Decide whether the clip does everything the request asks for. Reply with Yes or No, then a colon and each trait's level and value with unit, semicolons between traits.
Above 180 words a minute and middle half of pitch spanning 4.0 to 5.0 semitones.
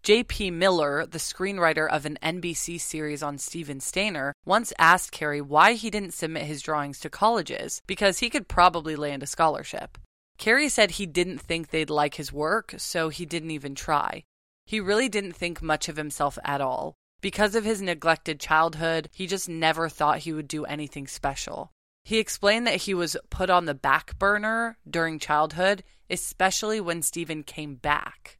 No: average, 175 wpm; average, 4.3 semitones